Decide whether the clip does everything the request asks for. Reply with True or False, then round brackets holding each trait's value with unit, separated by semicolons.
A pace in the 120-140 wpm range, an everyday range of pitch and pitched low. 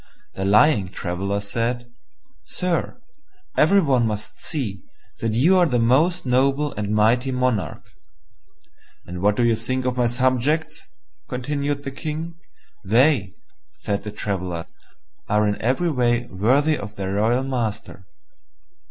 True (135 wpm; 4.9 semitones; 120 Hz)